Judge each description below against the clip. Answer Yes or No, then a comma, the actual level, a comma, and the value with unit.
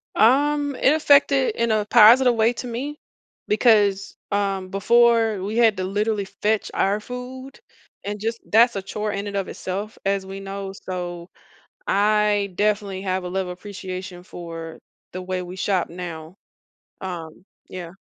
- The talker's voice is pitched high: Yes, high, 200 Hz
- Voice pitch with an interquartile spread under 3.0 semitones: No, average, 3.4 semitones